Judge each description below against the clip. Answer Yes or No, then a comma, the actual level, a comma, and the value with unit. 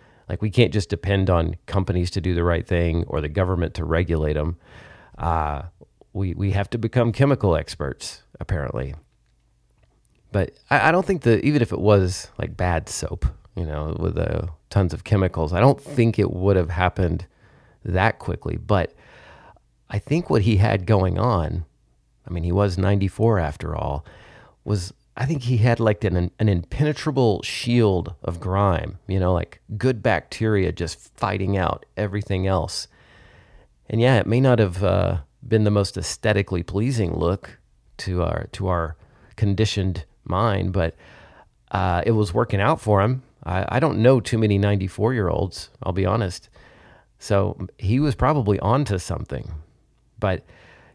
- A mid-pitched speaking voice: No, low, 100 Hz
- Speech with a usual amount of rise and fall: Yes, average, 4.2 semitones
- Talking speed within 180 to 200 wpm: No, average, 165 wpm